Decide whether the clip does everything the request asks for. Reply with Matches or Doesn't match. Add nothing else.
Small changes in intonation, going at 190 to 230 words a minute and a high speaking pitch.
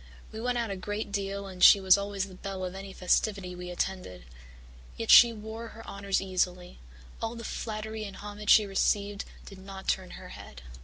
Matches